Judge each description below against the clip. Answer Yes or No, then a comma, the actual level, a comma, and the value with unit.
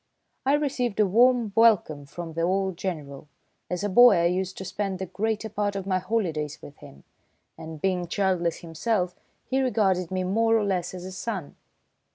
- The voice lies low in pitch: No, high, 190 Hz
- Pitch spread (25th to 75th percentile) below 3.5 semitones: No, average, 3.8 semitones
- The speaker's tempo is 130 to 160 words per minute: No, average, 185 wpm